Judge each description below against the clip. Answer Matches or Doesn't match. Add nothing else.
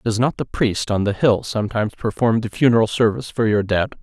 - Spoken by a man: Matches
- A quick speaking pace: Matches